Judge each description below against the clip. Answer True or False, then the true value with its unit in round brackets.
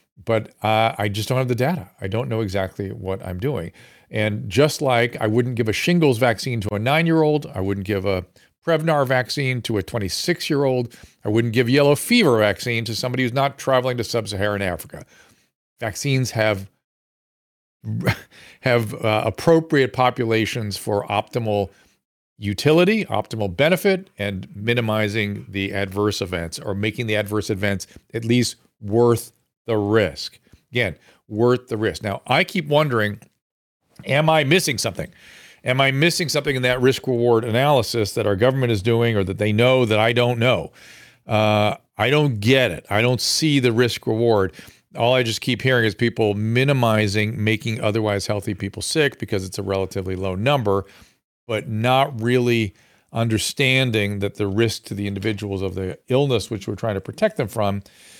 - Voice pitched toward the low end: True (115 Hz)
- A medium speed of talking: True (170 wpm)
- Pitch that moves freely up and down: False (3.8 semitones)